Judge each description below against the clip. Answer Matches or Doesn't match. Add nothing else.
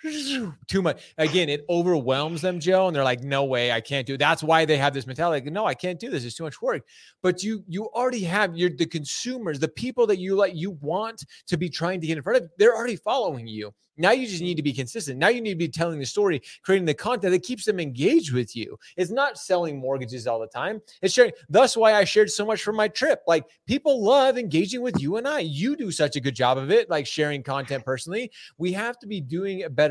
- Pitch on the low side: Doesn't match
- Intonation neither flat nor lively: Doesn't match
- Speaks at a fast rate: Matches